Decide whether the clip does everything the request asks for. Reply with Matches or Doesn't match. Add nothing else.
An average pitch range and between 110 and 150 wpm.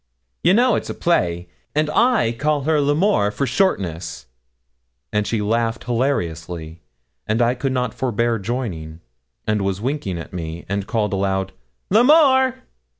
Doesn't match